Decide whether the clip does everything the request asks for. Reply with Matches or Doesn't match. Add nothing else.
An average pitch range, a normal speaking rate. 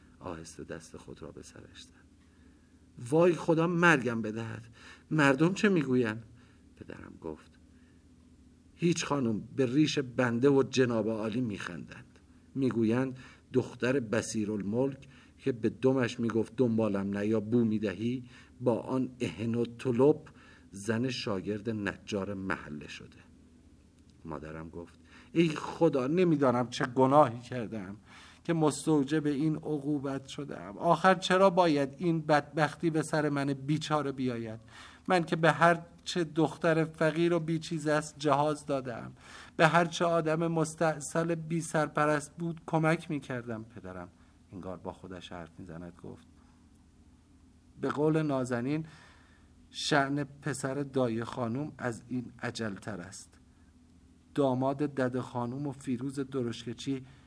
Doesn't match